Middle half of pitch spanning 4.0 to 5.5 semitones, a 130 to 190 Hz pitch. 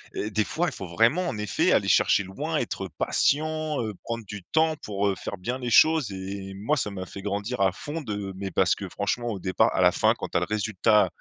No: average, 4.6 semitones; low, 105 Hz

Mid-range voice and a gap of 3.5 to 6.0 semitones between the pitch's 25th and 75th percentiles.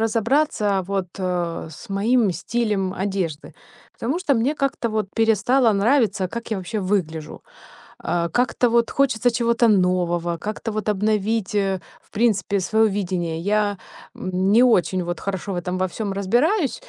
No: high, 205 Hz; average, 3.9 semitones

